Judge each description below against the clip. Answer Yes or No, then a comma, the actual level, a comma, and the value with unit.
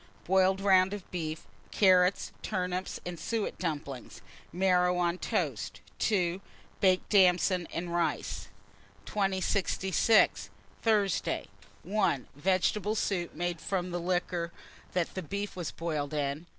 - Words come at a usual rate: No, slow, 110 wpm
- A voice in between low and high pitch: Yes, medium, 180 Hz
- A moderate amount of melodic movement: No, narrow, 2.0 semitones